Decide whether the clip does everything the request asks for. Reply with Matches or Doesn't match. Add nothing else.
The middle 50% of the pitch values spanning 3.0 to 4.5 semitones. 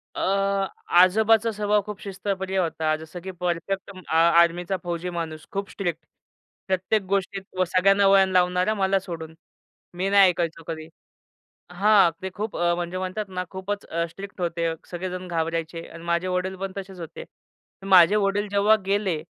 Doesn't match